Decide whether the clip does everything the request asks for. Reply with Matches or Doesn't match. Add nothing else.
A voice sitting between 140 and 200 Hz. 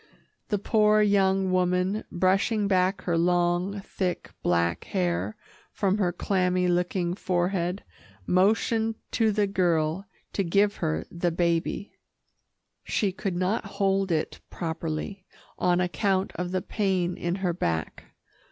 Matches